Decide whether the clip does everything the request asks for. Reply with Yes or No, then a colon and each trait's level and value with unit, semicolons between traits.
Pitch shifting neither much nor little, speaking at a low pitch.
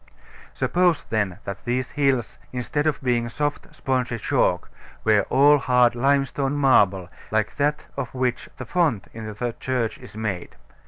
Yes: average, 4.0 semitones; low, 125 Hz